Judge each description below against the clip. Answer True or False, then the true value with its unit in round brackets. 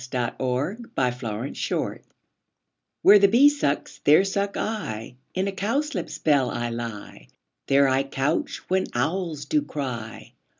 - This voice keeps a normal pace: False (130 wpm)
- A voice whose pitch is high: False (145 Hz)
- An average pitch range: False (8.0 semitones)